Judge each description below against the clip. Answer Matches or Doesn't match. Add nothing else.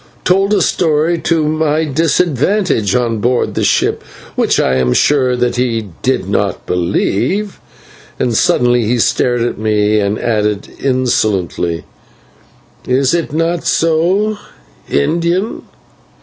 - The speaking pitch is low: Matches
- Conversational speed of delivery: Doesn't match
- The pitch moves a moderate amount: Doesn't match